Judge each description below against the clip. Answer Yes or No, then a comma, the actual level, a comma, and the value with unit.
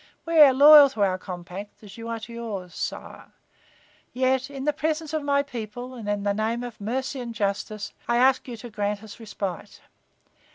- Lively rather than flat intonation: No, average, 4.3 semitones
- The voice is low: No, high, 235 Hz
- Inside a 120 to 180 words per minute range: No, average, 195 wpm